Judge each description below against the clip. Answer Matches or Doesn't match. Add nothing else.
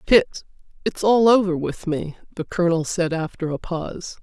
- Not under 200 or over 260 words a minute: Doesn't match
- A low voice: Doesn't match